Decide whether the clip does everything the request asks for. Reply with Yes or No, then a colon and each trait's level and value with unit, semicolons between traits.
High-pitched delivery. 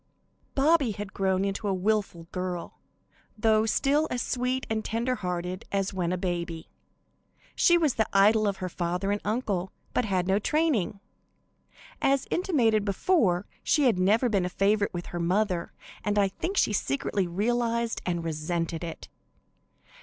Yes: high, 200 Hz